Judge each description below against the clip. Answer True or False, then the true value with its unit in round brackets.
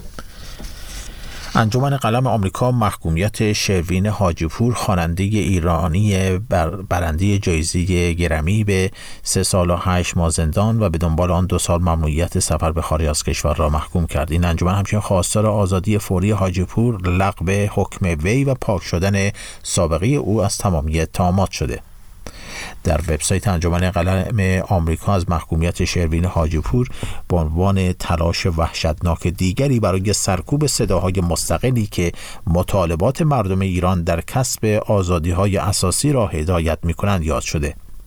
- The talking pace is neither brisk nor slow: True (135 wpm)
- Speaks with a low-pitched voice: True (95 Hz)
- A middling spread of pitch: True (3.3 semitones)